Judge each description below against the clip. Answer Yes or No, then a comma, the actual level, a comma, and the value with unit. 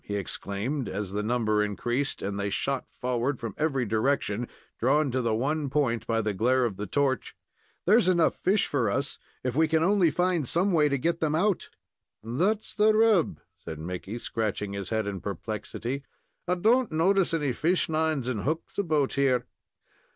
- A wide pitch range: Yes, wide, 6.7 semitones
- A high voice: No, low, 135 Hz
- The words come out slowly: No, average, 175 wpm